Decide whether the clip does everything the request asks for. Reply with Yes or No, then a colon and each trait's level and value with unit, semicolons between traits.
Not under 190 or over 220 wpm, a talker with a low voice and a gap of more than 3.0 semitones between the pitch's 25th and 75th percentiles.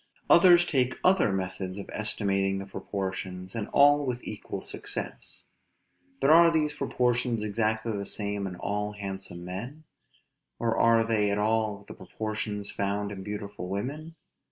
No: average, 145 wpm; low, 105 Hz; average, 3.6 semitones